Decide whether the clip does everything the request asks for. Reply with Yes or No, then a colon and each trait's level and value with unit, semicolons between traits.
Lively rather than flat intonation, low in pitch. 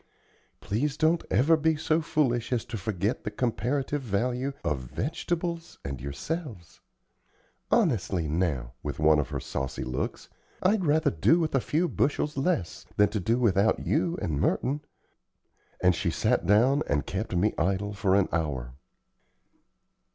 Yes: wide, 8.9 semitones; low, 115 Hz